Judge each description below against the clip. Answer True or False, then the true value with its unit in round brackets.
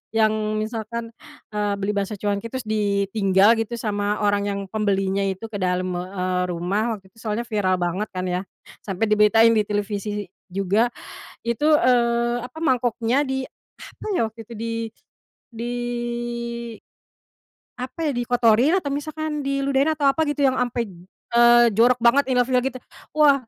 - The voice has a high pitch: True (225 Hz)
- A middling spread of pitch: True (3.4 semitones)